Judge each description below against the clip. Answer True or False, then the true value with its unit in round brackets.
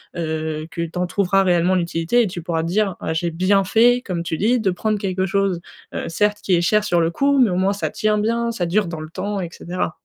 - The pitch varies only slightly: False (3.6 semitones)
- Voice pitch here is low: False (185 Hz)